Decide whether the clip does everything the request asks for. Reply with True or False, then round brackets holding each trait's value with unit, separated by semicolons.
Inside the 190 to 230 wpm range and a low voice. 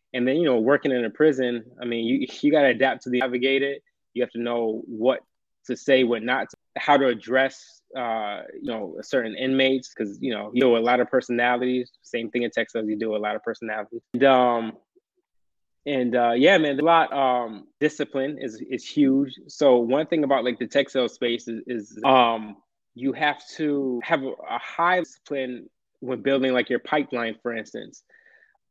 True (200 wpm; 125 Hz)